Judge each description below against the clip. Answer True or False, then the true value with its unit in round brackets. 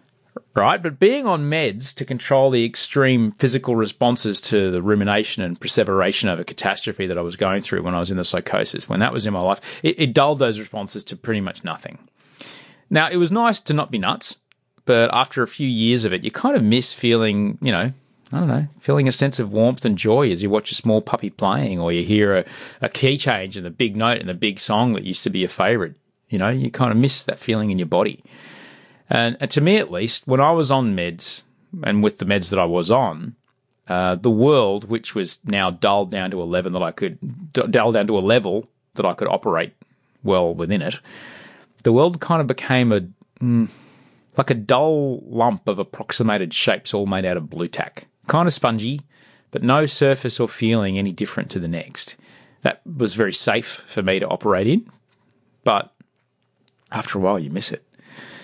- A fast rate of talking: True (215 wpm)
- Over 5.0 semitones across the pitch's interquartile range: True (5.4 semitones)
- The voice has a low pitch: True (115 Hz)